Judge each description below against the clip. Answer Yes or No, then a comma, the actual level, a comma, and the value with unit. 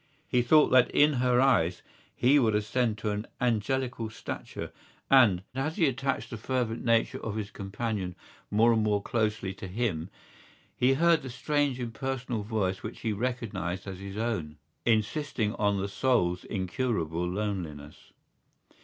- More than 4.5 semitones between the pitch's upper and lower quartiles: No, average, 4.2 semitones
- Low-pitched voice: Yes, low, 110 Hz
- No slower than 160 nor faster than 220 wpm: No, average, 150 wpm